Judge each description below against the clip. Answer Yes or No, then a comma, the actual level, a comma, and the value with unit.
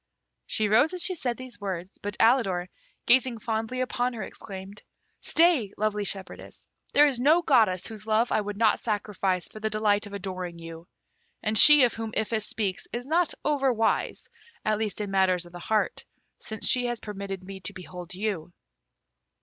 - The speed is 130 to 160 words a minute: No, average, 180 wpm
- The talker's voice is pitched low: No, high, 215 Hz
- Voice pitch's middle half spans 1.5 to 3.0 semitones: No, average, 3.8 semitones